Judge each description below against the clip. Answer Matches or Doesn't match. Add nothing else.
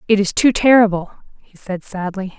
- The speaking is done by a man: Doesn't match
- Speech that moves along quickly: Doesn't match